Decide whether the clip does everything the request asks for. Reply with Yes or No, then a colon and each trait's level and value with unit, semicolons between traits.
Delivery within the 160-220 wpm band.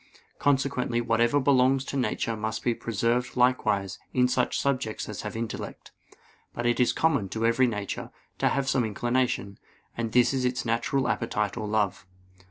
Yes: average, 165 wpm